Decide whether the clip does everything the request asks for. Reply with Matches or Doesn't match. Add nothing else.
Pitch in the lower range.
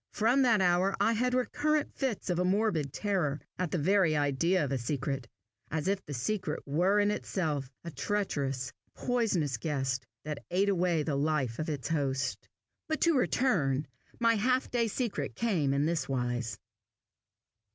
Doesn't match